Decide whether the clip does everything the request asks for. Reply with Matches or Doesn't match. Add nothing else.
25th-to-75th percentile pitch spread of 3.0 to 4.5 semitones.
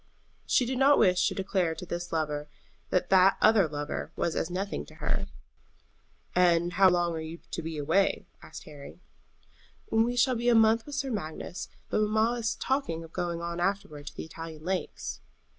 Doesn't match